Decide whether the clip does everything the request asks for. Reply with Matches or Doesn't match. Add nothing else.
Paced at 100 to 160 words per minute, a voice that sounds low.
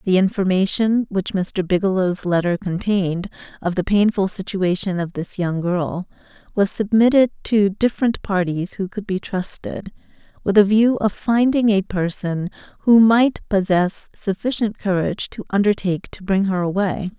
Doesn't match